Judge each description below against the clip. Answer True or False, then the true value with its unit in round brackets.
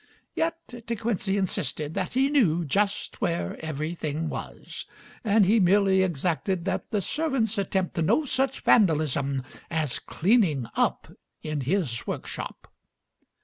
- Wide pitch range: True (6.0 semitones)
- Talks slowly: True (125 wpm)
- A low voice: False (190 Hz)